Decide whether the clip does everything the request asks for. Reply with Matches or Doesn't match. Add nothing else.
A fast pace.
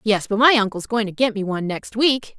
Matches